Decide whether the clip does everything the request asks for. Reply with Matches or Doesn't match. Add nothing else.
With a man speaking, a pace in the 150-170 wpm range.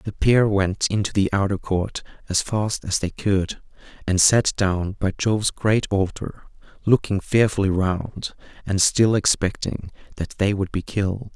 Matches